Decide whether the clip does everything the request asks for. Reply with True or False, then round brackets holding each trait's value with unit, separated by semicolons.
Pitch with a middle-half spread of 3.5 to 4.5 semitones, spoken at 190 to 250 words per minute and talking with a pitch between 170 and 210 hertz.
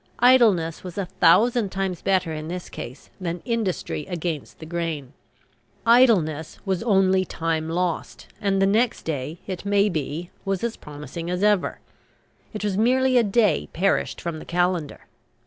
False (3.9 semitones; 155 wpm; 185 Hz)